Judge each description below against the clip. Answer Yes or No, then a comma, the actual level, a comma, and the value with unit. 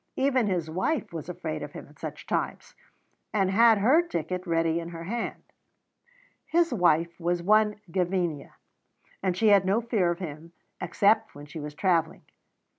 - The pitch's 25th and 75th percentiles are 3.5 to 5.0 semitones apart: Yes, average, 4.4 semitones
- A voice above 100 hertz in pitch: Yes, medium, 185 Hz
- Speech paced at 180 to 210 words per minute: No, average, 165 wpm